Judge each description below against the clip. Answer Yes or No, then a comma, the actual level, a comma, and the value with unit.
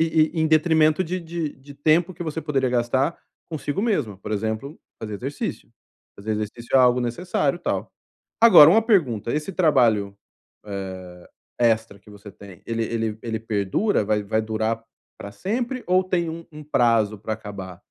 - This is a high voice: No, low, 125 Hz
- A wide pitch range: Yes, wide, 6.9 semitones